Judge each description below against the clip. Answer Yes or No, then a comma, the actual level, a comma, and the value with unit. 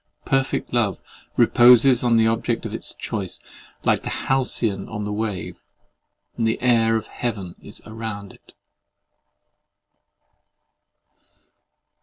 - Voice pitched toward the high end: No, low, 115 Hz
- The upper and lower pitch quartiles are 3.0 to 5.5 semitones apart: No, narrow, 2.5 semitones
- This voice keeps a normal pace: No, slow, 115 wpm